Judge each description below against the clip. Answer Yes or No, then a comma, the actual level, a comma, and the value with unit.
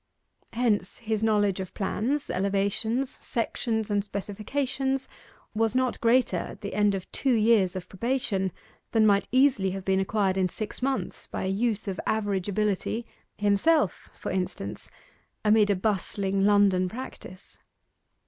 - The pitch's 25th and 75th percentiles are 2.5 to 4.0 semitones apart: Yes, average, 3.1 semitones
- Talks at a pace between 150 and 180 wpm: No, average, 140 wpm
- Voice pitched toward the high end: Yes, high, 205 Hz